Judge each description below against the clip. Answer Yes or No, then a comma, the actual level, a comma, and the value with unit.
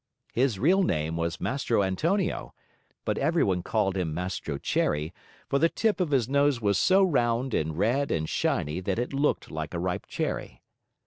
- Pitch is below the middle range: Yes, low, 110 Hz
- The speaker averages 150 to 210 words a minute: Yes, average, 175 wpm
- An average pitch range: No, wide, 8.5 semitones